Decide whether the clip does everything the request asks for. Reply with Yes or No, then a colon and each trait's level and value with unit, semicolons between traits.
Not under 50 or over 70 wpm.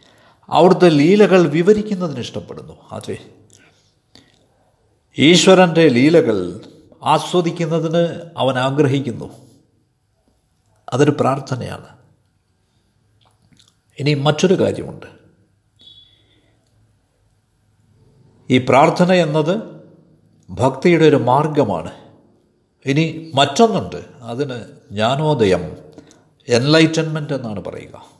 Yes: slow, 60 wpm